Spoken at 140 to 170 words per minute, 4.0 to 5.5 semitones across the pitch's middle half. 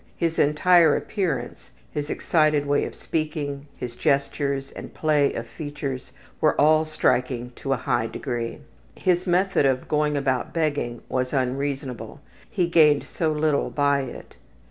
No: average, 145 wpm; average, 2.9 semitones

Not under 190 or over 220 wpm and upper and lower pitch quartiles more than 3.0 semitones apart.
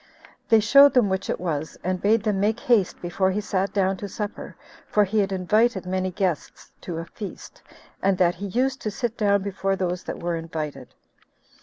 No: average, 195 wpm; average, 2.7 semitones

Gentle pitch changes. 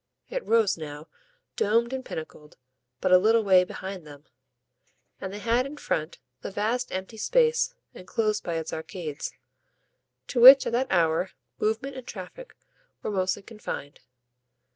No: average, 5.1 semitones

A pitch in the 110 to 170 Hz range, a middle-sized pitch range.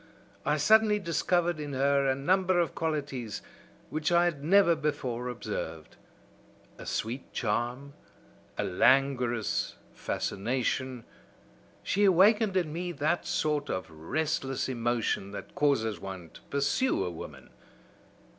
No: medium, 140 Hz; wide, 6.1 semitones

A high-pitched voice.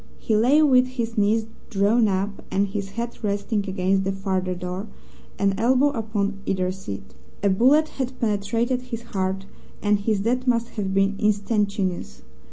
Yes: high, 205 Hz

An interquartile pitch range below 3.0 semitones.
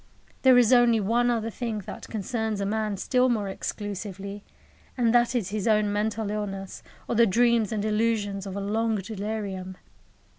Yes: narrow, 2.4 semitones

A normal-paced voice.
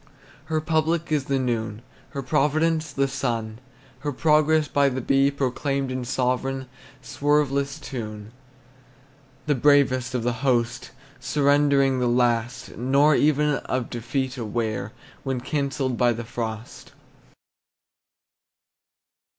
No: slow, 115 wpm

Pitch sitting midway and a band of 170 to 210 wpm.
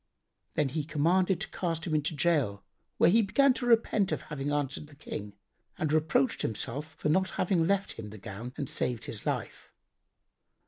Yes: medium, 155 Hz; average, 180 wpm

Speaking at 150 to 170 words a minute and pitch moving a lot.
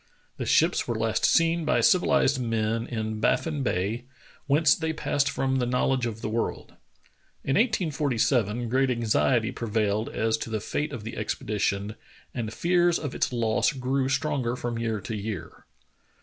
No: average, 165 wpm; average, 4.3 semitones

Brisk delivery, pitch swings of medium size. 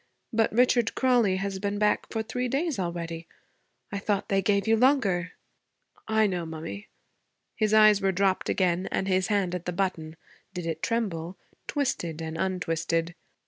No: average, 160 wpm; average, 4.1 semitones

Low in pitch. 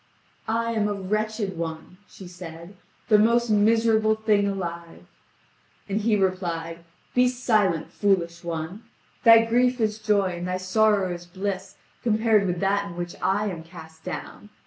No: high, 200 Hz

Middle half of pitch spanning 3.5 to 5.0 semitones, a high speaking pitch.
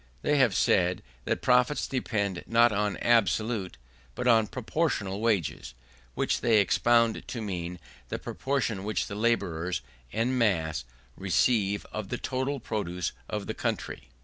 No: average, 4.0 semitones; low, 110 Hz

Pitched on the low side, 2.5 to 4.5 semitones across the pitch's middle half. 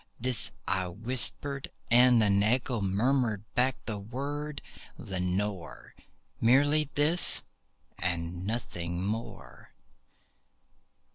No: low, 115 Hz; average, 5.3 semitones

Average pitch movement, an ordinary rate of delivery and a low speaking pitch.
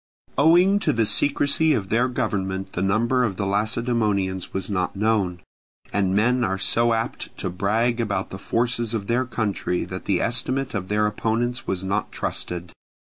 Yes: average, 3.8 semitones; average, 170 wpm; low, 110 Hz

